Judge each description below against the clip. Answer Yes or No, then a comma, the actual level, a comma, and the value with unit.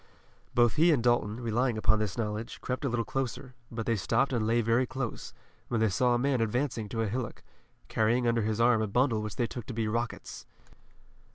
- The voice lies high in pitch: No, low, 115 Hz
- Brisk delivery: Yes, fast, 210 wpm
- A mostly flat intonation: Yes, narrow, 2.2 semitones